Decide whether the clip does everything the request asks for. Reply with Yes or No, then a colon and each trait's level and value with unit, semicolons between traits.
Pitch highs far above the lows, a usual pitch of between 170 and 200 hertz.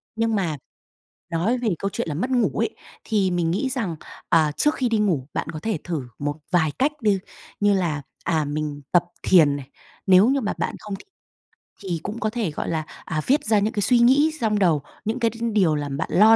Yes: wide, 5.9 semitones; high, 195 Hz